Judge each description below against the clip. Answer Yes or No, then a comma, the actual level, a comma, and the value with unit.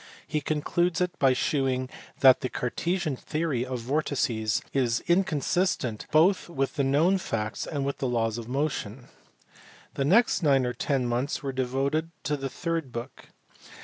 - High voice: No, low, 135 Hz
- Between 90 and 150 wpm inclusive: No, average, 160 wpm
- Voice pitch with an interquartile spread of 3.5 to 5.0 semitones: Yes, average, 4.0 semitones